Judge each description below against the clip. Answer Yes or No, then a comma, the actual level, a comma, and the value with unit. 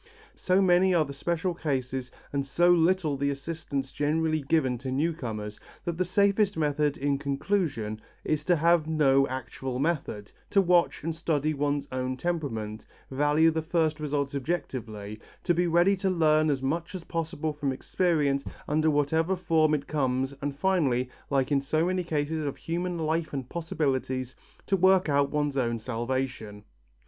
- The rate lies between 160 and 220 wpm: Yes, average, 165 wpm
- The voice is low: No, medium, 150 Hz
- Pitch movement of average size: Yes, average, 3.8 semitones